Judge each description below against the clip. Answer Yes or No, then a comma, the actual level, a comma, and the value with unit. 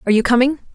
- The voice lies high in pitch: Yes, very high, 250 Hz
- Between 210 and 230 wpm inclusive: No, fast, 240 wpm